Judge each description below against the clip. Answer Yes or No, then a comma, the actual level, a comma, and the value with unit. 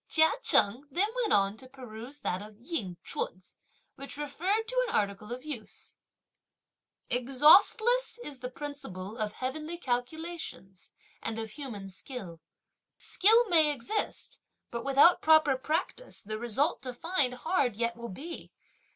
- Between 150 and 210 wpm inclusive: No, average, 140 wpm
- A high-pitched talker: Yes, very high, 265 Hz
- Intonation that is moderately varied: No, wide, 6.4 semitones